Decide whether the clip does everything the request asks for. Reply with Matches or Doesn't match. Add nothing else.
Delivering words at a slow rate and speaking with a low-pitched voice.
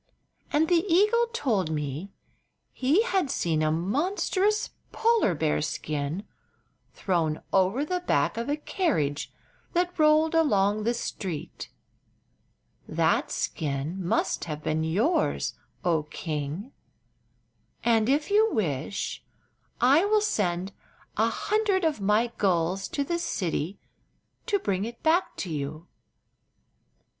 Doesn't match